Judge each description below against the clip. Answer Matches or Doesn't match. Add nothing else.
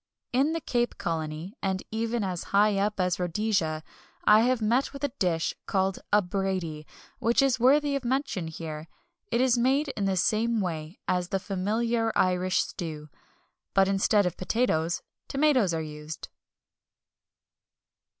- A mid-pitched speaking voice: Doesn't match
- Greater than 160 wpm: Doesn't match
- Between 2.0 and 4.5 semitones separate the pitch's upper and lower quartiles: Doesn't match